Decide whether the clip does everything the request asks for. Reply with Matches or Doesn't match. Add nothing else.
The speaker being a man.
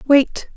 Doesn't match